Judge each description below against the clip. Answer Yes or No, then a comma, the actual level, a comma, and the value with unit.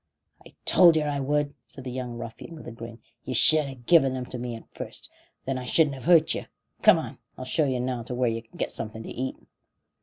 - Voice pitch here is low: Yes, low, 130 Hz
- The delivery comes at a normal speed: No, fast, 245 wpm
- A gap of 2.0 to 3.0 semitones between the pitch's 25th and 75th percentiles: No, average, 3.4 semitones